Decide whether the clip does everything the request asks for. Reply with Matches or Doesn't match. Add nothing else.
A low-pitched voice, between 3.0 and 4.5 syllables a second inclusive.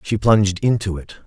Doesn't match